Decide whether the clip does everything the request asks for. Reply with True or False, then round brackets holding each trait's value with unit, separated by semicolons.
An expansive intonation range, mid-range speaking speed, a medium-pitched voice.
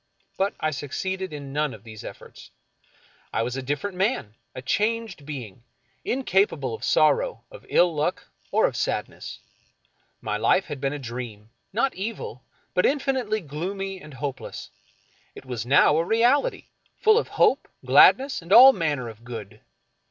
True (8.4 semitones; 155 wpm; 155 Hz)